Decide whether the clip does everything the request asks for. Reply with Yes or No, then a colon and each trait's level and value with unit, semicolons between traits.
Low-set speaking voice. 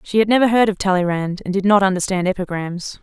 No: high, 190 Hz